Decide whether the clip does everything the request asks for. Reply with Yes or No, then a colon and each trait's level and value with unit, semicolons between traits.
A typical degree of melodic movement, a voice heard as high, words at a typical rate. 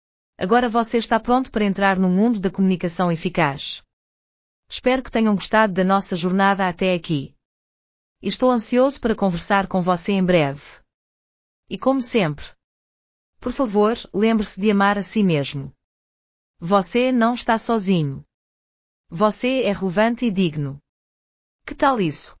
No: wide, 7.5 semitones; high, 195 Hz; average, 140 wpm